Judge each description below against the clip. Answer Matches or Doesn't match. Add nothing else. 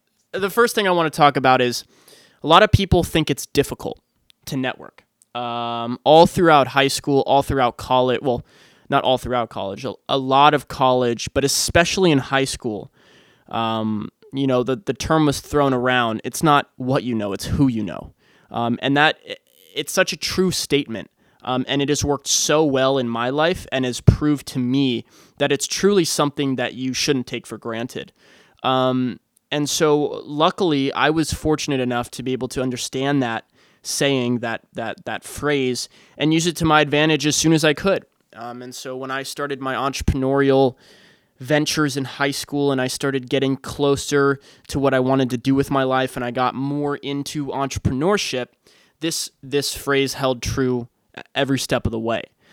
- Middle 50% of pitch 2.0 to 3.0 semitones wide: Matches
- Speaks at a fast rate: Doesn't match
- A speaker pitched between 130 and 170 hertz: Matches